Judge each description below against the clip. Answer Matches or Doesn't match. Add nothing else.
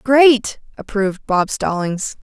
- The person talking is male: Doesn't match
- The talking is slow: Matches